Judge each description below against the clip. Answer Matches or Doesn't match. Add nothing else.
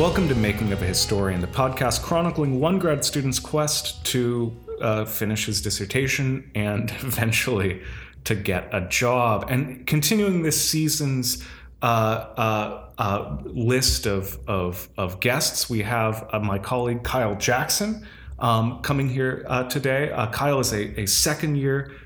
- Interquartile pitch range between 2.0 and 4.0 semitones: Doesn't match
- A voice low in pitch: Matches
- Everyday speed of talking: Matches